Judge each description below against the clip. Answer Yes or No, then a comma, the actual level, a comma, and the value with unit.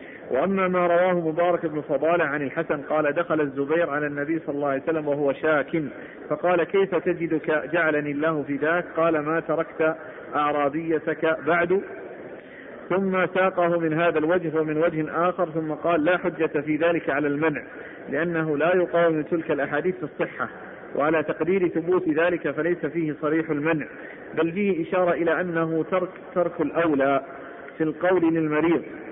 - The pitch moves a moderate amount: No, narrow, 2.0 semitones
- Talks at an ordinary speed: No, fast, 150 wpm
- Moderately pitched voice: Yes, medium, 160 Hz